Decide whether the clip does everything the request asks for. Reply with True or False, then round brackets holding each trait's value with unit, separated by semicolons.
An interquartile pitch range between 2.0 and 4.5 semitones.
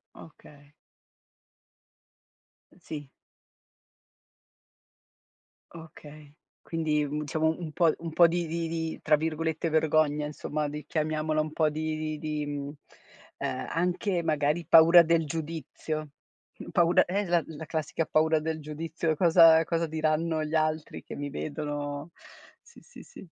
False (1.4 semitones)